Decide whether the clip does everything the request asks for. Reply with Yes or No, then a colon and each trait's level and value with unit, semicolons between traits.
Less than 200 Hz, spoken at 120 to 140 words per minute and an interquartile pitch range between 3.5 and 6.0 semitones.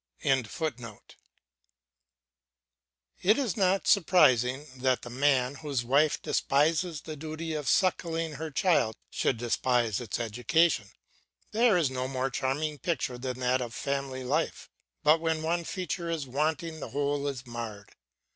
Yes: medium, 140 Hz; slow, 135 wpm; average, 4.3 semitones